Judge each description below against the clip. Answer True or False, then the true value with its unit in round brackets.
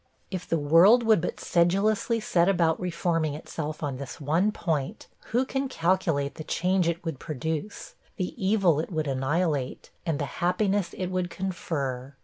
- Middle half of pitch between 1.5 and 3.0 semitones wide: False (3.8 semitones)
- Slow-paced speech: False (160 wpm)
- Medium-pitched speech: True (170 Hz)